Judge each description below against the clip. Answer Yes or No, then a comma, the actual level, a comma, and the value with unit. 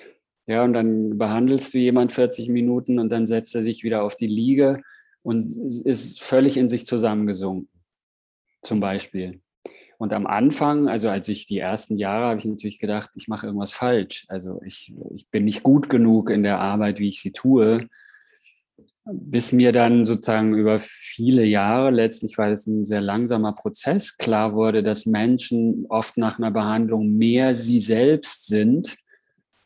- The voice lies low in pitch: Yes, low, 115 Hz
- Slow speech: No, average, 165 wpm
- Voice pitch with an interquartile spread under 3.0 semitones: Yes, narrow, 2.5 semitones